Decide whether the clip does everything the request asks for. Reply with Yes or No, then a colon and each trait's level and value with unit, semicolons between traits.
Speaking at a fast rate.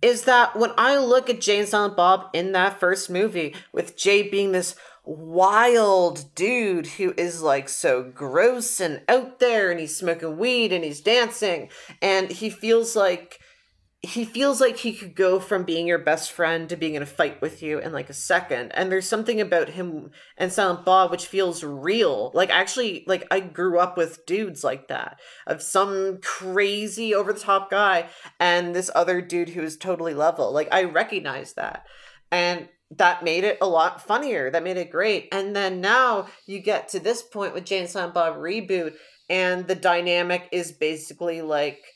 No: average, 185 wpm